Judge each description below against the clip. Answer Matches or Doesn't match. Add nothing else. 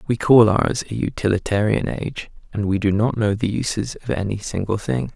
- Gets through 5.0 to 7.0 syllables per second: Matches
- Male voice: Matches